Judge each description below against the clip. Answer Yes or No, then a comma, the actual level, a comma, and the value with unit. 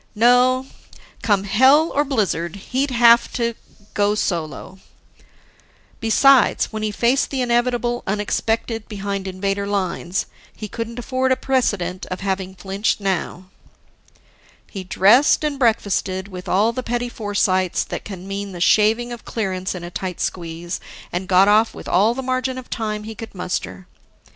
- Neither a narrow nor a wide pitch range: Yes, average, 4.2 semitones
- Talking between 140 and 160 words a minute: Yes, average, 150 wpm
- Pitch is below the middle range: No, high, 210 Hz